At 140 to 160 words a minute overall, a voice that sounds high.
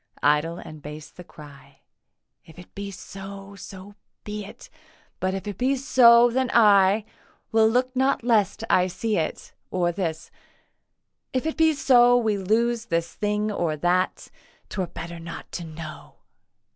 Yes: average, 155 wpm; high, 195 Hz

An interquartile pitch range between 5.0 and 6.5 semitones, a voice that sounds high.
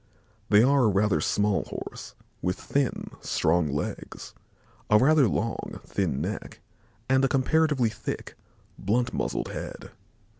No: wide, 5.5 semitones; low, 110 Hz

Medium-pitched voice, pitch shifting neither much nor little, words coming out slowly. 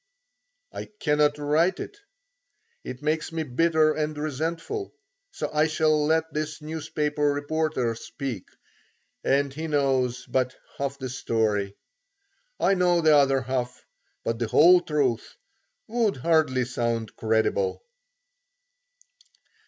Yes: medium, 150 Hz; average, 3.7 semitones; slow, 115 wpm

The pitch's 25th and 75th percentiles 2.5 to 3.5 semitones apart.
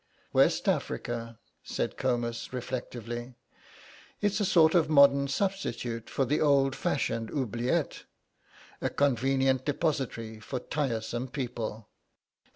Yes: average, 3.1 semitones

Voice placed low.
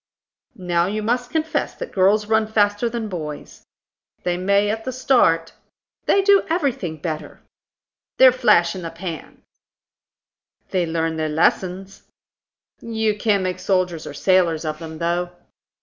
No: high, 190 Hz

